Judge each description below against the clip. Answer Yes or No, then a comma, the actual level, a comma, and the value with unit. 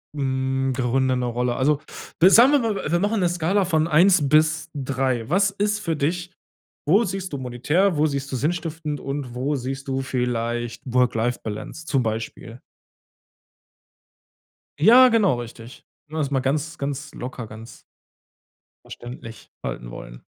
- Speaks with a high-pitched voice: No, medium, 140 Hz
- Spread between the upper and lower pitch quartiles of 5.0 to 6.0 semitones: Yes, wide, 5.5 semitones